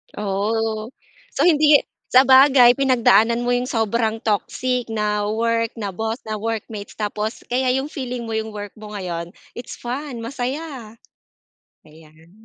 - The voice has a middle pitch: No, high, 225 Hz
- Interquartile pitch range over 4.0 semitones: No, average, 3.0 semitones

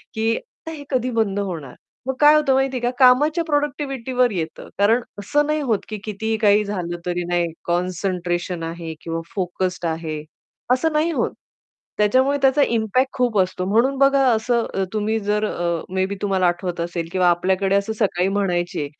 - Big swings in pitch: Yes, wide, 6.4 semitones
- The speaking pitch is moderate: No, high, 210 Hz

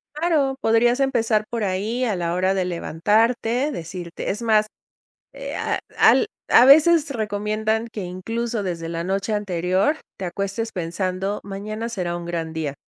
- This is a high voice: Yes, high, 210 Hz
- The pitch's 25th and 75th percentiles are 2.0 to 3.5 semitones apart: No, average, 4.3 semitones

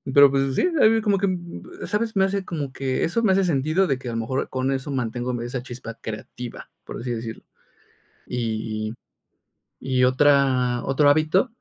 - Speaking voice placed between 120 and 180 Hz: Yes, low, 135 Hz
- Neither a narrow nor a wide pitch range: No, wide, 6.0 semitones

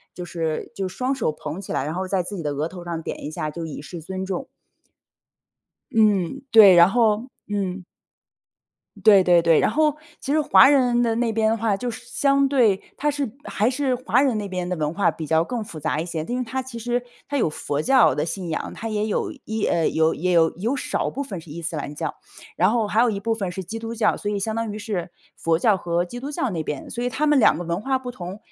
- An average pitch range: No, wide, 6.0 semitones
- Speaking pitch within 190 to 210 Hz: Yes, high, 205 Hz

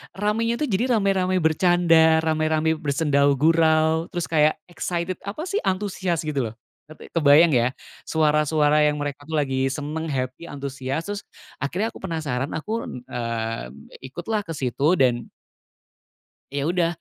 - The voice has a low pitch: No, medium, 160 Hz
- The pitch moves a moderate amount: Yes, average, 3.7 semitones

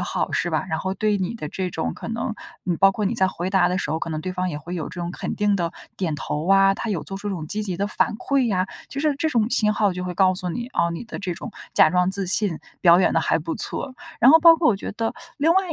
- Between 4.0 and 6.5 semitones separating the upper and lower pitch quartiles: No, average, 3.6 semitones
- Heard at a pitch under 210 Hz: Yes, high, 190 Hz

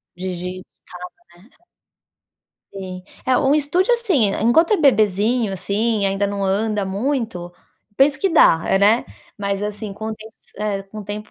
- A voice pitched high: Yes, high, 210 Hz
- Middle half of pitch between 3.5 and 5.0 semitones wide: Yes, average, 4.0 semitones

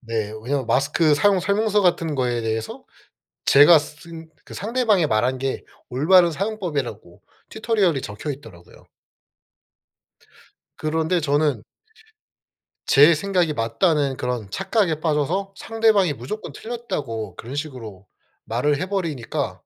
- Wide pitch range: Yes, wide, 6.7 semitones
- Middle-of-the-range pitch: Yes, medium, 150 Hz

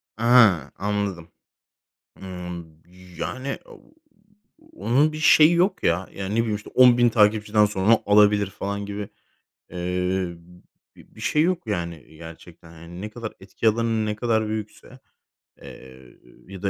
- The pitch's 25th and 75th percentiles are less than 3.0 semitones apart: No, average, 4.2 semitones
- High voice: No, low, 105 Hz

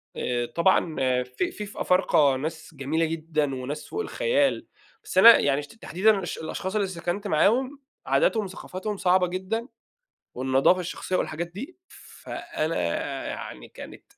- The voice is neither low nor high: Yes, medium, 180 Hz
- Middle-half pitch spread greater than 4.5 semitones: Yes, average, 5.0 semitones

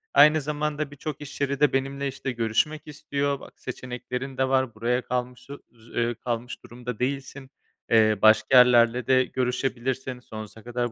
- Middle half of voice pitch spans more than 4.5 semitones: No, narrow, 2.5 semitones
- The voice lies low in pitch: Yes, low, 130 Hz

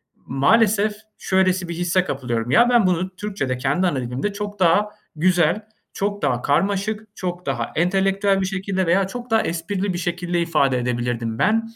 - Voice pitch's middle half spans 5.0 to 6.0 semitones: Yes, wide, 5.6 semitones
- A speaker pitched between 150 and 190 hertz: Yes, medium, 185 Hz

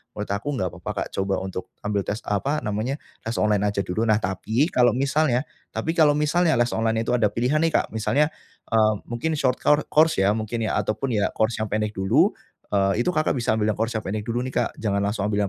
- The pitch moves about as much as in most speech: Yes, average, 4.6 semitones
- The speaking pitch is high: No, low, 110 Hz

